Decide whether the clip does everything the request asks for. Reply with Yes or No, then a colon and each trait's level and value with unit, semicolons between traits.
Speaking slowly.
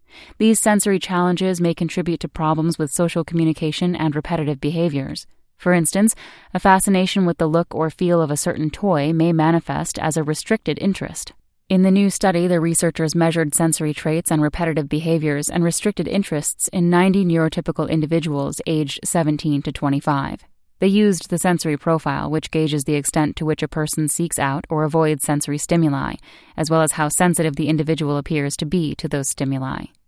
No: average, 175 wpm